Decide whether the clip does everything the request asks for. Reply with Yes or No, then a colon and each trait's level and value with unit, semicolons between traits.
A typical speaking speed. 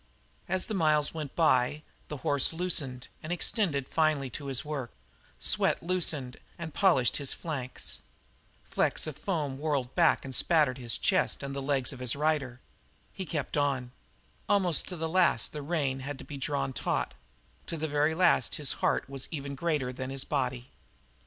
Yes: average, 170 wpm